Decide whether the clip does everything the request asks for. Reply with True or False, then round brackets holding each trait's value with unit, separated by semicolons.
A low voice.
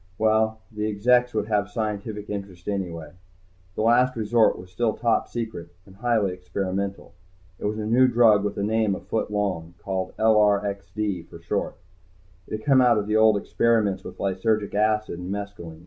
True (105 Hz)